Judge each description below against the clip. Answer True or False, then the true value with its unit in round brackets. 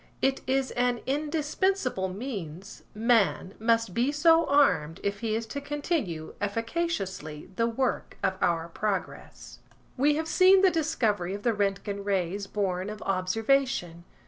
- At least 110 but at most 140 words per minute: True (135 wpm)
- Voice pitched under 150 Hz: False (225 Hz)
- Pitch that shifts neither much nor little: False (6.7 semitones)